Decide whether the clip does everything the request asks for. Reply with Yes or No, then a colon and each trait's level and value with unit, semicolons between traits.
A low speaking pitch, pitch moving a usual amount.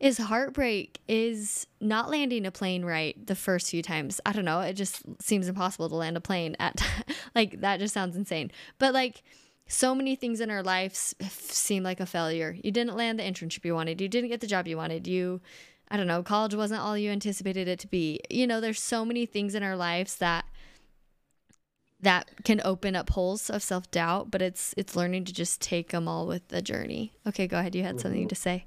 No: high, 190 Hz; average, 3.4 semitones